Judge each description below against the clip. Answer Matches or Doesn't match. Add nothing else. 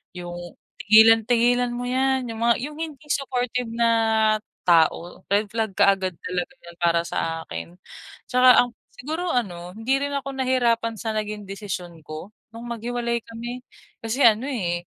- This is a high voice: Matches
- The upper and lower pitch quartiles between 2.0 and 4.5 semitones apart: Doesn't match